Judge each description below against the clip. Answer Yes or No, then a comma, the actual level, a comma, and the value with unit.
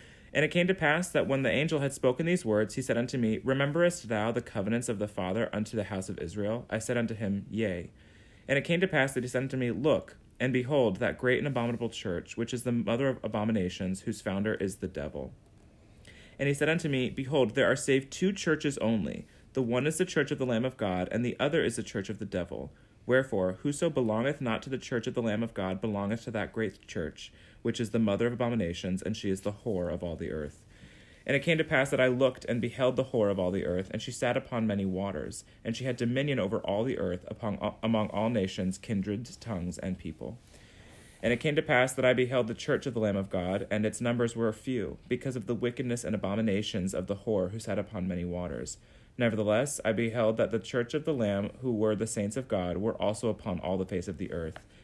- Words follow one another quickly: Yes, fast, 240 wpm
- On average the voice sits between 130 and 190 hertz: No, low, 115 Hz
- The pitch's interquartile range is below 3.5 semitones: No, average, 4.2 semitones